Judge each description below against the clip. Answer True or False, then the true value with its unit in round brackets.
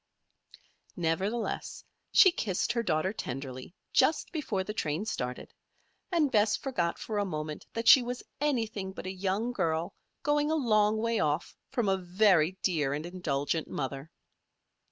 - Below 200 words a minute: True (150 wpm)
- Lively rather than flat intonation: True (6.4 semitones)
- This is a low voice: False (190 Hz)